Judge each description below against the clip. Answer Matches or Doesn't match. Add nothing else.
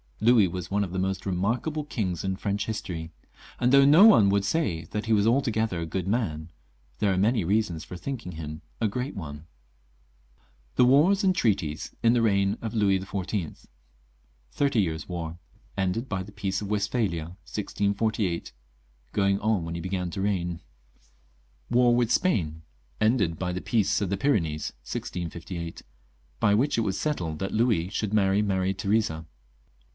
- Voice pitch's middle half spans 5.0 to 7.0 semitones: Doesn't match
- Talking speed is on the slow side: Doesn't match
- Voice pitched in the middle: Doesn't match